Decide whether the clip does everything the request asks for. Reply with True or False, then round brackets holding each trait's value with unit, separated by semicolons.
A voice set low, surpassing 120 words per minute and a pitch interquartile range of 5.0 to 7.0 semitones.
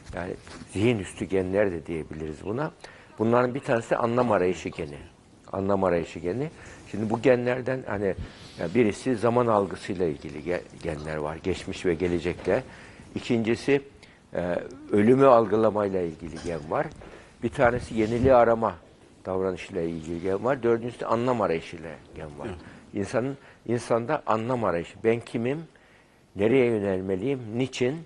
True (105 Hz; 130 wpm; 5.3 semitones)